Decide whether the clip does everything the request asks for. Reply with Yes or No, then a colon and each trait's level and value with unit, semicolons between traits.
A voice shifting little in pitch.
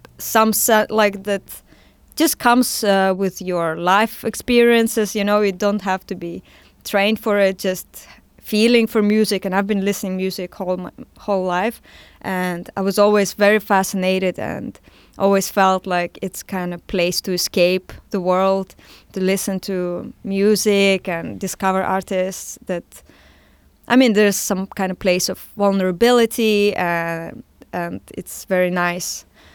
Yes: narrow, 2.2 semitones